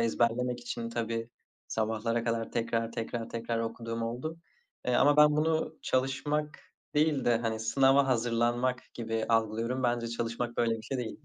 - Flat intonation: Yes, narrow, 2.0 semitones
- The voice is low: Yes, low, 120 Hz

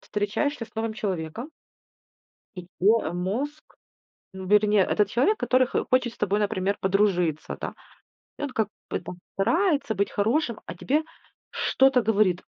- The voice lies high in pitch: Yes, high, 215 Hz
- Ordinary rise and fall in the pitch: Yes, average, 4.6 semitones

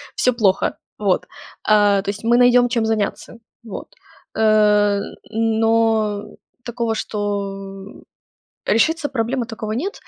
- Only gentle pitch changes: Yes, narrow, 2.2 semitones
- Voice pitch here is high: Yes, high, 220 Hz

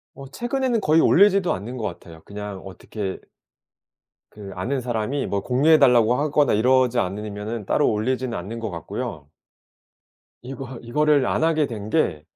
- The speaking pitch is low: Yes, low, 120 Hz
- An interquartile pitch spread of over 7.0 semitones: No, wide, 5.7 semitones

